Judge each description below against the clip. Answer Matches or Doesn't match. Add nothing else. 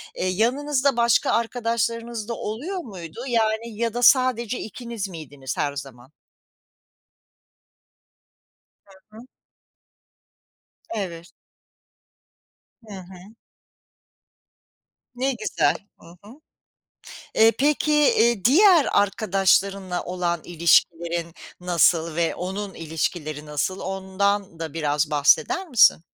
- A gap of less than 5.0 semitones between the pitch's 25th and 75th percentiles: Doesn't match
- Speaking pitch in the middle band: Doesn't match